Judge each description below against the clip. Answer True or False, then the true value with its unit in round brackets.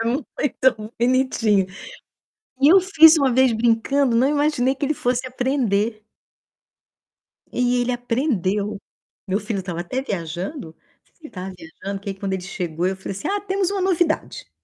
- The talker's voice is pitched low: False (245 Hz)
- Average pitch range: False (6.0 semitones)